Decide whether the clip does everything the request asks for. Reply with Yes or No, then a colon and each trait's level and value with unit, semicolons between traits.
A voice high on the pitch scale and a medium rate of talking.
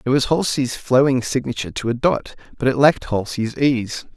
No: low, 130 Hz; average, 190 wpm